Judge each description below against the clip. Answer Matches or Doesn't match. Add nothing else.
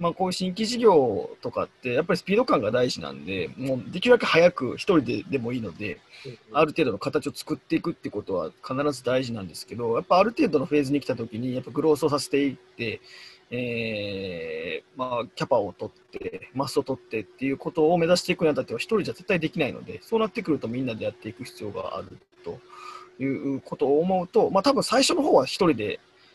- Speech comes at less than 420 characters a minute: Doesn't match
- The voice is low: Doesn't match